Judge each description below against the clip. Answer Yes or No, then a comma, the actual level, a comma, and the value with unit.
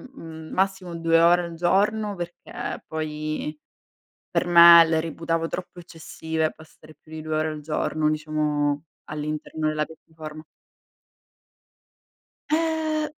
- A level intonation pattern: Yes, narrow, 2.1 semitones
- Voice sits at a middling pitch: Yes, medium, 160 Hz